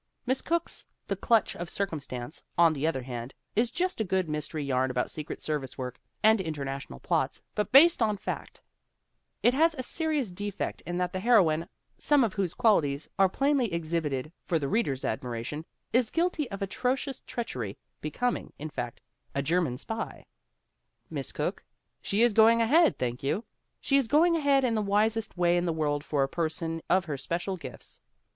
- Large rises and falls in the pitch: Yes, wide, 7.9 semitones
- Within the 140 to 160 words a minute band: No, average, 180 wpm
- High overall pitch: No, medium, 180 Hz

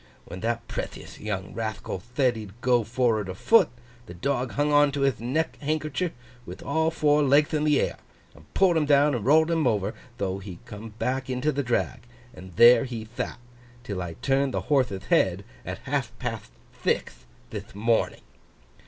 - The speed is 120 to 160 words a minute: No, average, 180 wpm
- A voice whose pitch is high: No, low, 125 Hz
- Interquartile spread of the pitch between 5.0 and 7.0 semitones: Yes, wide, 5.4 semitones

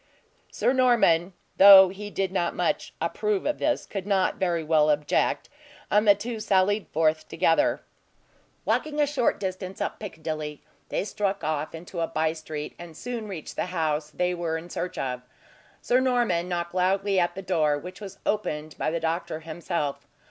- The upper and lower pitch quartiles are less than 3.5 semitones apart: No, average, 4.0 semitones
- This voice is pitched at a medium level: Yes, medium, 180 Hz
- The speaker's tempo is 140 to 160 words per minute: No, average, 170 wpm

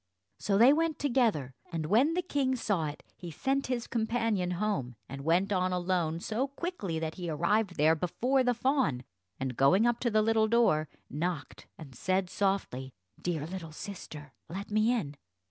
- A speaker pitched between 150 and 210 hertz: Yes, high, 190 Hz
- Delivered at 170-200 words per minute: Yes, average, 175 wpm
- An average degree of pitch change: No, wide, 6.8 semitones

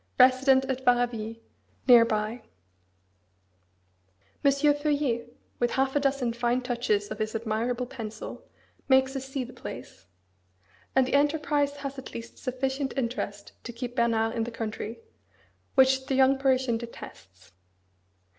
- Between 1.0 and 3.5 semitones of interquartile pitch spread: Yes, narrow, 2.6 semitones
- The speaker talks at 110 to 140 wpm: Yes, slow, 135 wpm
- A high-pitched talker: Yes, very high, 250 Hz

